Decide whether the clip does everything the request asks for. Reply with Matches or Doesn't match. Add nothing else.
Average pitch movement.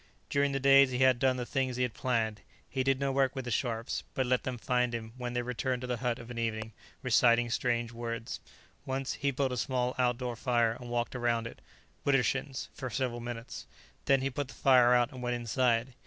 Doesn't match